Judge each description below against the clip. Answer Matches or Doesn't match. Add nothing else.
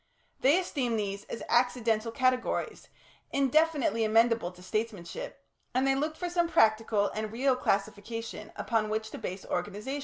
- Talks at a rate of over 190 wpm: Doesn't match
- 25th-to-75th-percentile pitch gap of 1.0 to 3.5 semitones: Doesn't match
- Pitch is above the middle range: Matches